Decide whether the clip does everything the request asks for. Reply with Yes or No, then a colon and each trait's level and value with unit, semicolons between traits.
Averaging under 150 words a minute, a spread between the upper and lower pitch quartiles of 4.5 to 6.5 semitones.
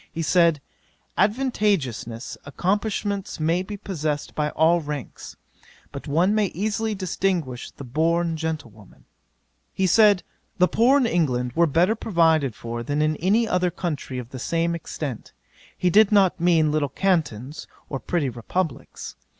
Yes: average, 140 wpm; average, 4.9 semitones